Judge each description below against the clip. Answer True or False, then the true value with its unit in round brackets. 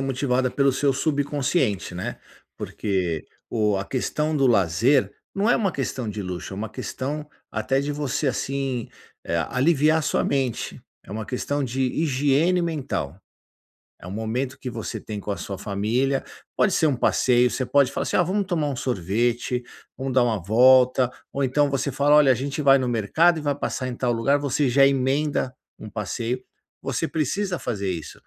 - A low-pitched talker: True (130 Hz)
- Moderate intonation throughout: True (3.8 semitones)